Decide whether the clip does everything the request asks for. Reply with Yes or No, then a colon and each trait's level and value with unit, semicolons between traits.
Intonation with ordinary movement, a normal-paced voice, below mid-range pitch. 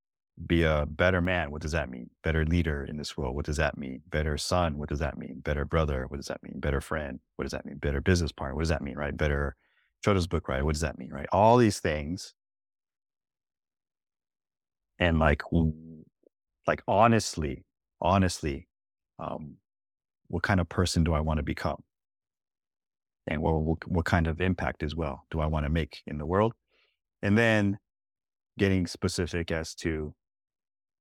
Yes: average, 3.2 semitones; average, 180 wpm; very low, 80 Hz